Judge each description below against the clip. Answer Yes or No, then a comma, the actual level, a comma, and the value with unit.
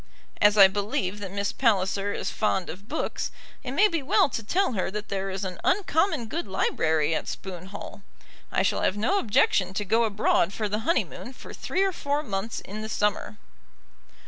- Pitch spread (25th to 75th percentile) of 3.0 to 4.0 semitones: No, average, 4.5 semitones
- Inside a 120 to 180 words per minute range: No, average, 195 wpm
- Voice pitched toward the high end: Yes, high, 205 Hz